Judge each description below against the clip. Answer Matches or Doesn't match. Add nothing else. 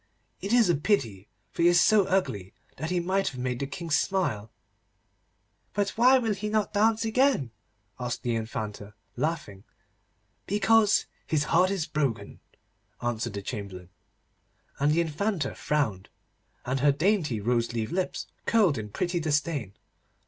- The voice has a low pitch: Doesn't match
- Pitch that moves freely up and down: Matches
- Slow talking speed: Doesn't match